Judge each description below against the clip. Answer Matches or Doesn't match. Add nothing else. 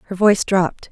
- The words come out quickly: Doesn't match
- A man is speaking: Doesn't match